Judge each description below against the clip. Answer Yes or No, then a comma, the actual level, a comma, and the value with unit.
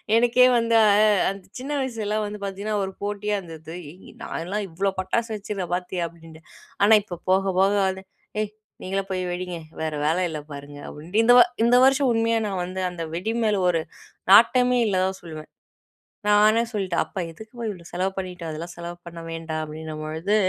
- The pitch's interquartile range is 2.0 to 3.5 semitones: No, average, 3.9 semitones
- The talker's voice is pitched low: No, high, 190 Hz